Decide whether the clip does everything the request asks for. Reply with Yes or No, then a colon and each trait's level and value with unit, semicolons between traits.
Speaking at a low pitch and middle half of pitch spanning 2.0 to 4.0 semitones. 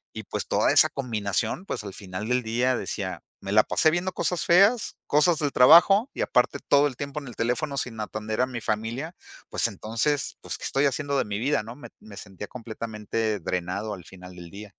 No: low, 115 Hz; wide, 5.4 semitones